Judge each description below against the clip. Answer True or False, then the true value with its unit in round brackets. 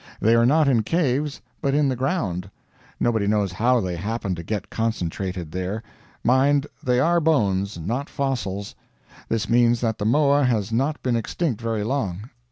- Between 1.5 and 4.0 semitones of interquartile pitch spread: False (5.1 semitones)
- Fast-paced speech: False (170 wpm)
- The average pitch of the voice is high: False (115 Hz)